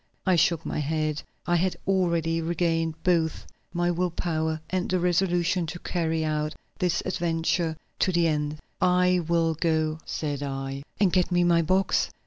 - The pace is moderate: Yes, average, 160 wpm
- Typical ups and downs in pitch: No, narrow, 2.0 semitones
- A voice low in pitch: No, medium, 170 Hz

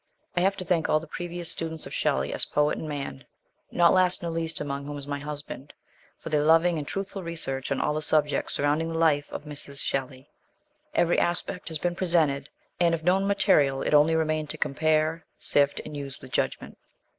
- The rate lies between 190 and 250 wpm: Yes, fast, 205 wpm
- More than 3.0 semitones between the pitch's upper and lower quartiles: No, average, 2.7 semitones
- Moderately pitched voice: Yes, medium, 155 Hz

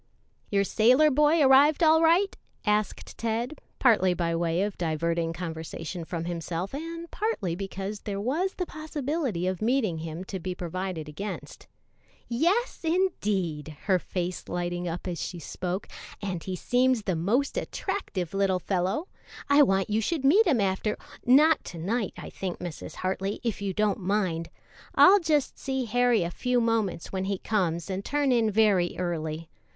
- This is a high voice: Yes, high, 200 Hz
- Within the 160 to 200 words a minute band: Yes, average, 165 wpm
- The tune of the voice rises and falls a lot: Yes, wide, 7.0 semitones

